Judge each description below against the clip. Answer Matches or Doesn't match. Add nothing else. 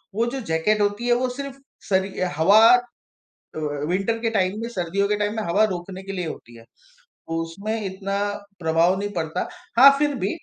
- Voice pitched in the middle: Doesn't match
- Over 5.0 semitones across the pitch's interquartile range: Doesn't match